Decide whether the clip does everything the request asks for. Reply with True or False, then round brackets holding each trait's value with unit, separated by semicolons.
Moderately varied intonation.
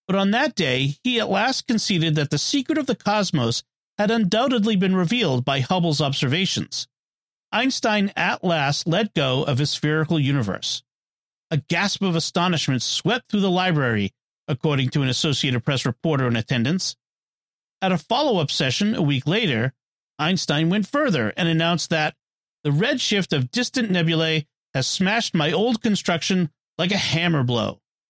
False (5.8 semitones)